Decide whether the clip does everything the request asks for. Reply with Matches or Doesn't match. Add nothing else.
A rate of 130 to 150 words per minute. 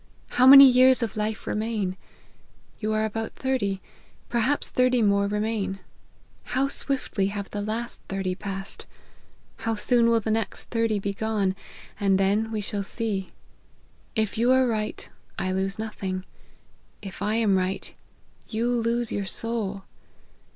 Matches